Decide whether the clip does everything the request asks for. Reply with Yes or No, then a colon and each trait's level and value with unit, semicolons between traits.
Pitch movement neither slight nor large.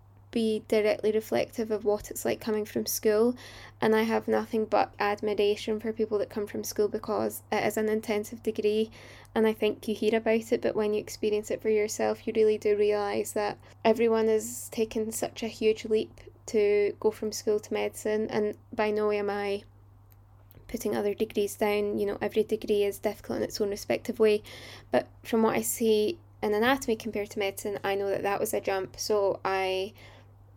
No: narrow, 1.3 semitones